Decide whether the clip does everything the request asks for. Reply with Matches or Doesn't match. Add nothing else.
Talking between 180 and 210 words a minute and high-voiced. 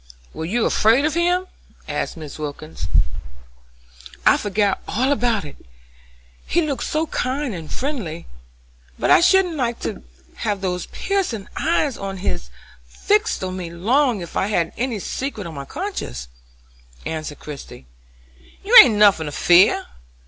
Doesn't match